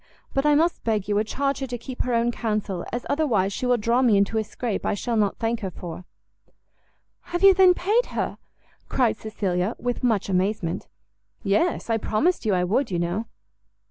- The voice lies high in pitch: Yes, high, 225 Hz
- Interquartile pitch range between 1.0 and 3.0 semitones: No, average, 4.4 semitones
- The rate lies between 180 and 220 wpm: Yes, average, 200 wpm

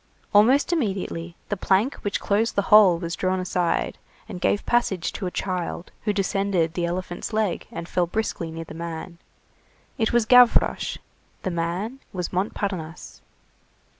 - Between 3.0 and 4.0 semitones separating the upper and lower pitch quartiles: Yes, average, 3.7 semitones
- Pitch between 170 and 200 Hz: Yes, medium, 185 Hz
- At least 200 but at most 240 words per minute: No, average, 150 wpm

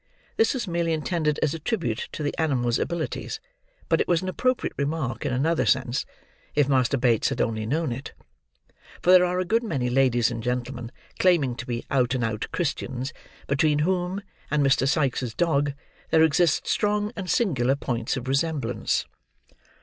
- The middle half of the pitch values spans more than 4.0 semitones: Yes, wide, 5.5 semitones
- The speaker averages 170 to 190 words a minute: Yes, average, 175 wpm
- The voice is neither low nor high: Yes, medium, 145 Hz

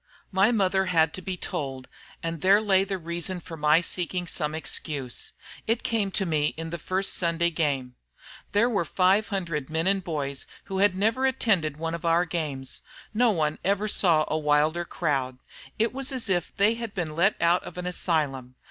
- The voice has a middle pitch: Yes, medium, 175 Hz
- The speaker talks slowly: No, average, 190 wpm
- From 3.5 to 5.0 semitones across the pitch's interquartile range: Yes, average, 4.1 semitones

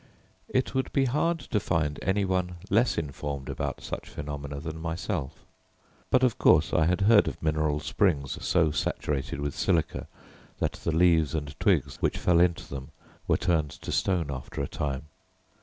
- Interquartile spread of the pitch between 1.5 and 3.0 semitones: No, average, 4.4 semitones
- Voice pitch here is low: Yes, very low, 80 Hz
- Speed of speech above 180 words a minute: No, average, 170 wpm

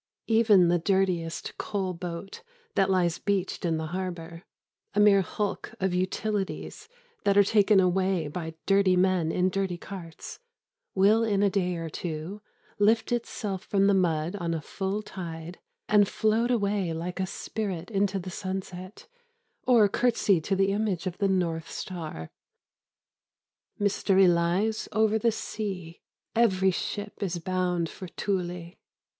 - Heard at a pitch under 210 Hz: Yes, high, 190 Hz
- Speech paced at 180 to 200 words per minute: No, average, 145 wpm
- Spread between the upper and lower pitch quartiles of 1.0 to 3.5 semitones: Yes, average, 2.7 semitones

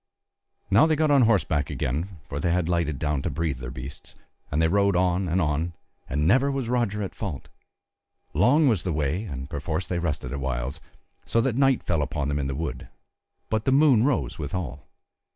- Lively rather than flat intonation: Yes, wide, 7.0 semitones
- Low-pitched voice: Yes, very low, 85 Hz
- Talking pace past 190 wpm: Yes, average, 200 wpm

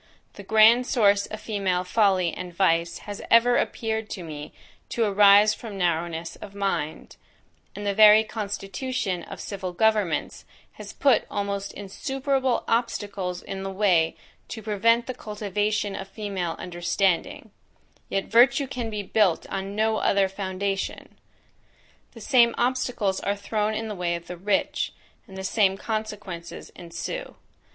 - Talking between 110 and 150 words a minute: Yes, average, 145 wpm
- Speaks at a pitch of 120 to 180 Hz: No, high, 200 Hz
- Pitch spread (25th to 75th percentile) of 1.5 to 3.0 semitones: Yes, average, 2.7 semitones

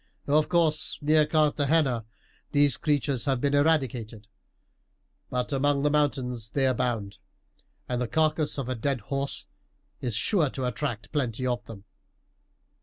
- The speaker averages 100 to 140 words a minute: Yes, slow, 135 wpm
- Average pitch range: Yes, average, 3.4 semitones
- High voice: No, low, 135 Hz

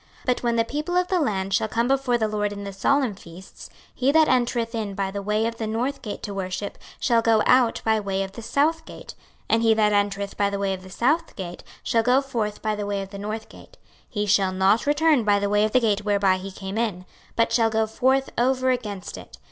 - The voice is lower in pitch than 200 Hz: No, high, 215 Hz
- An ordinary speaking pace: No, fast, 250 wpm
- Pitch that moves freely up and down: No, average, 3.6 semitones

